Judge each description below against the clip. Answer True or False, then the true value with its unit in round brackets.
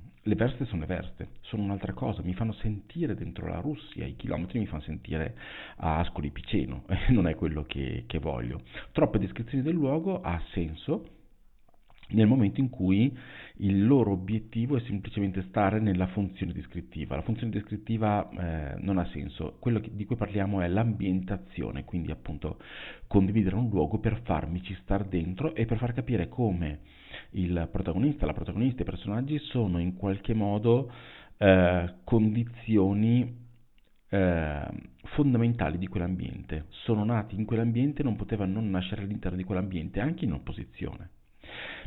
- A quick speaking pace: False (150 wpm)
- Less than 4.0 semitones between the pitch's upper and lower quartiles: False (4.4 semitones)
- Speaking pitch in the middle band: False (100 Hz)